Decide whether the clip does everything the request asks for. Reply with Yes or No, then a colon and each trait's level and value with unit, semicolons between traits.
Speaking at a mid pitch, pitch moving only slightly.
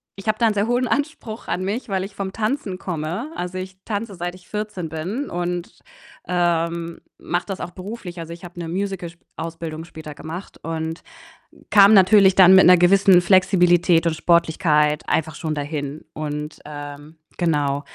No: medium, 175 Hz; average, 3.3 semitones